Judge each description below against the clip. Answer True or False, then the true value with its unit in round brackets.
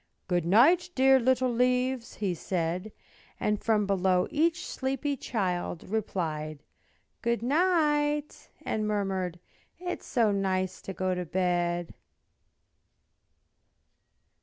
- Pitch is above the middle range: True (210 Hz)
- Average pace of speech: False (110 wpm)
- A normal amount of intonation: False (6.4 semitones)